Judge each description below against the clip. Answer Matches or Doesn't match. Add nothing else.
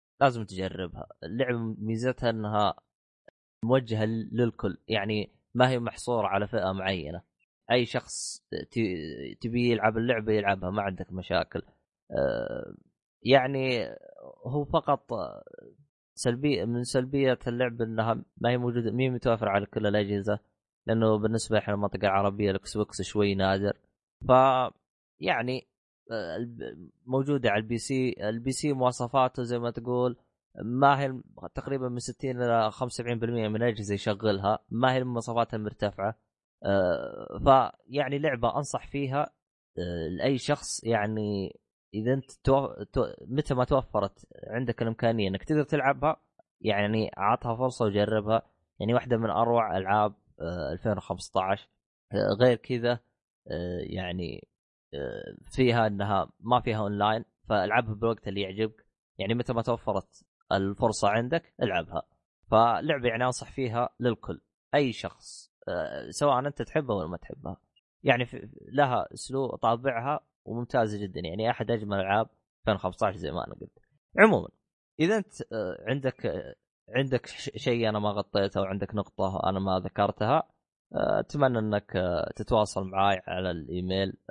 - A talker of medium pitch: Doesn't match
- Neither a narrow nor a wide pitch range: Matches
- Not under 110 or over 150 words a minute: Matches